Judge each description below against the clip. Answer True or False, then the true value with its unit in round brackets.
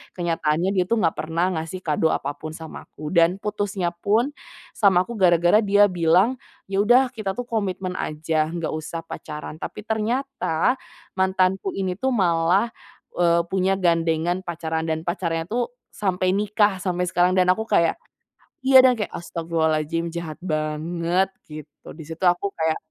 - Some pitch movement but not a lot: True (3.5 semitones)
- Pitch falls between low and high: True (180 Hz)